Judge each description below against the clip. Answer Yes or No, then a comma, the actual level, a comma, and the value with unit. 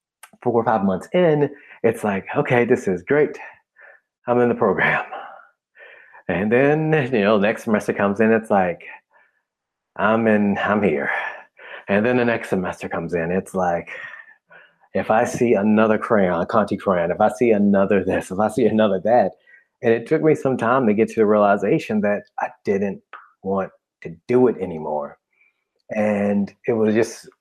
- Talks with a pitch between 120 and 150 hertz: No, low, 110 Hz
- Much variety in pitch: No, average, 3.6 semitones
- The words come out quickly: No, average, 175 wpm